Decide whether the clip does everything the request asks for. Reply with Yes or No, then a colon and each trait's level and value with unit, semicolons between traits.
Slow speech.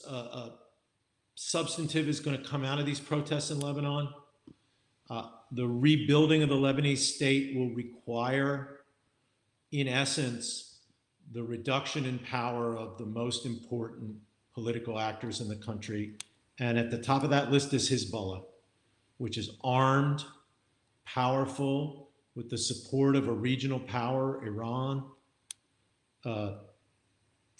Yes: slow, 130 wpm